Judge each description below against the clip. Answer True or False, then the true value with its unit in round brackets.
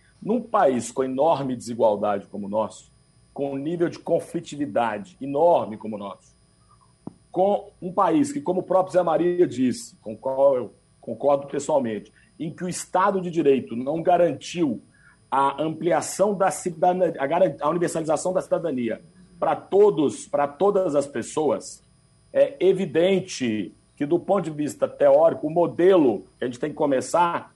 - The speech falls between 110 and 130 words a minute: False (155 wpm)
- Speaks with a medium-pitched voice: True (170 Hz)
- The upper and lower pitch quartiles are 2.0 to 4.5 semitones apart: False (5.4 semitones)